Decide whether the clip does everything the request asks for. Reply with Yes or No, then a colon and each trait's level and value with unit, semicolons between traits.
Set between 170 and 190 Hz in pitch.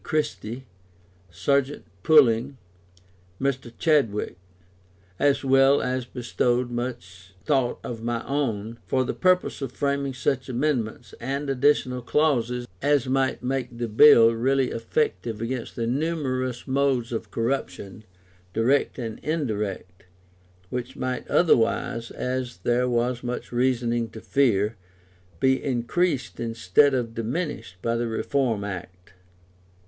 No: low, 125 Hz